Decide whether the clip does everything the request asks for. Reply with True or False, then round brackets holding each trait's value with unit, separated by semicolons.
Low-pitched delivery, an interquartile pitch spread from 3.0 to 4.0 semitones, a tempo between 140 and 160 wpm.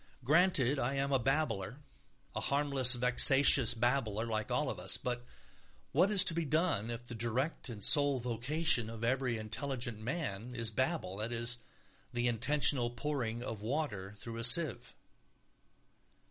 True (125 Hz; 3.6 semitones; 150 wpm)